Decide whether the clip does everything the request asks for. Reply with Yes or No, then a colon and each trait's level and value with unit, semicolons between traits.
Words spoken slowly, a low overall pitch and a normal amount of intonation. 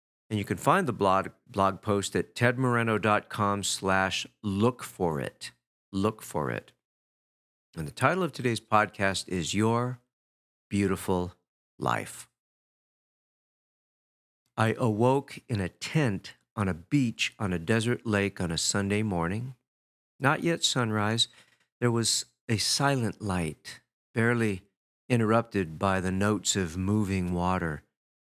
Yes: slow, 125 wpm; low, 100 Hz; average, 4.2 semitones